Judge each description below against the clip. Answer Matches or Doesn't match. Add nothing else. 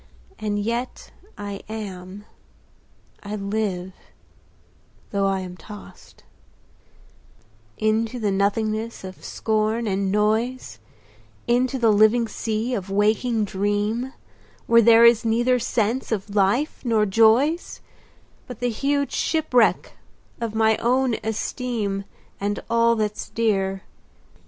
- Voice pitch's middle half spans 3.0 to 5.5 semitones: Doesn't match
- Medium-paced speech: Doesn't match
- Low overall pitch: Doesn't match